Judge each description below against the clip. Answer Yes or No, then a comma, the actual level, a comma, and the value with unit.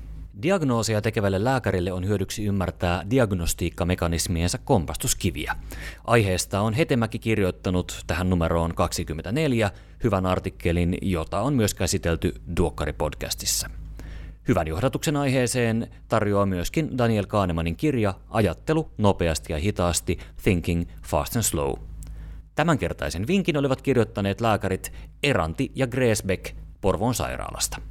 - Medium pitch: No, very low, 95 Hz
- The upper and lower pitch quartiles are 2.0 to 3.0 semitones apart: No, average, 5.0 semitones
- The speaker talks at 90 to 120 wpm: Yes, average, 105 wpm